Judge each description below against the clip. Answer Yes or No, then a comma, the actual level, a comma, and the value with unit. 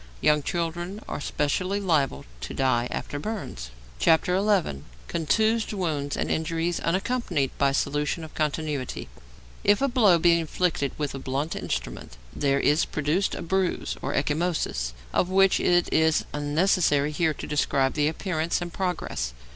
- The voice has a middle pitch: Yes, medium, 160 Hz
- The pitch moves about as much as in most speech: Yes, average, 4.1 semitones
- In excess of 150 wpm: No, average, 145 wpm